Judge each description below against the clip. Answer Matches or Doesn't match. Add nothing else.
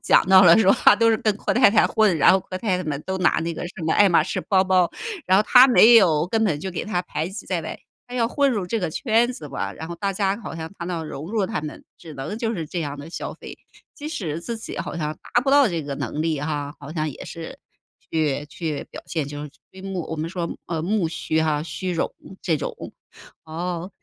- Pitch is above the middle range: Doesn't match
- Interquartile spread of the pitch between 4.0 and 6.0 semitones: Matches